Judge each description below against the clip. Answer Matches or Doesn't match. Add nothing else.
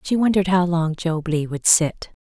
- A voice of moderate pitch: Matches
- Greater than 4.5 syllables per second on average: Matches